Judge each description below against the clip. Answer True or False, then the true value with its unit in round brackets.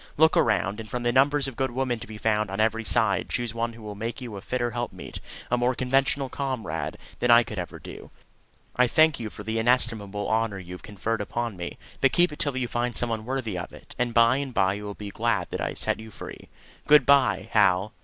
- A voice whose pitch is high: False (115 Hz)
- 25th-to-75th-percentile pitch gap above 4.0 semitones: False (3.2 semitones)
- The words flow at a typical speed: False (245 wpm)